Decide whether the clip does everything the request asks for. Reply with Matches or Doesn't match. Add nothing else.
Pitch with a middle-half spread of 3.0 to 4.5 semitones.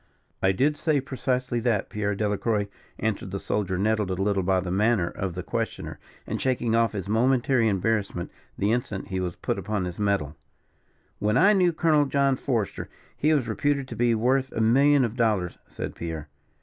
Doesn't match